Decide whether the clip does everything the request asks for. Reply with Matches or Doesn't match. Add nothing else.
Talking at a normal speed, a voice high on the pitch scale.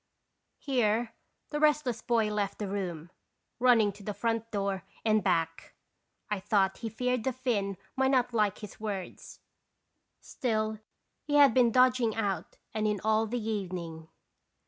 Matches